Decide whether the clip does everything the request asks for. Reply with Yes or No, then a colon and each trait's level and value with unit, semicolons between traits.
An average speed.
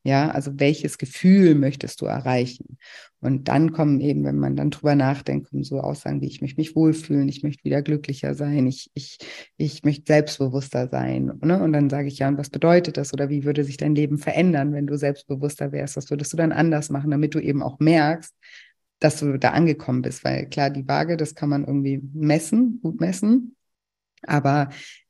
No: fast, 200 wpm